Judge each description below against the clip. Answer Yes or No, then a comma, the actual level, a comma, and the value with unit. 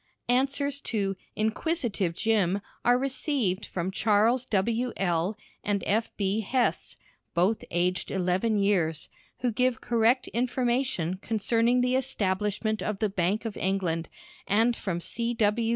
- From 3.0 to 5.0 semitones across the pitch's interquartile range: Yes, average, 4.1 semitones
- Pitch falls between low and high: No, high, 215 Hz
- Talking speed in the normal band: No, slow, 130 wpm